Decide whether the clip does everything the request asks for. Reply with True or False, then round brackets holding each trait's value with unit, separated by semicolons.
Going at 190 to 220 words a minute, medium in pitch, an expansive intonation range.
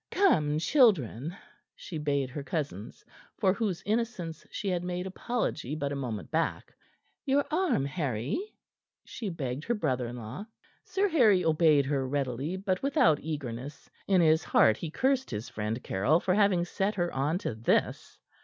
False (160 wpm; 160 Hz; 6.5 semitones)